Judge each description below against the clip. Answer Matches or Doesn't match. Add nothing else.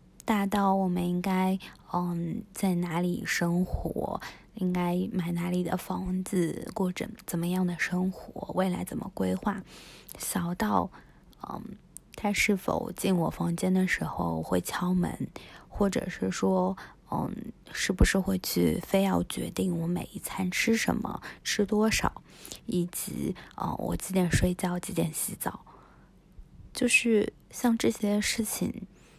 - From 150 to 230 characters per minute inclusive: Matches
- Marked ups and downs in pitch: Doesn't match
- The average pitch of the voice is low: Doesn't match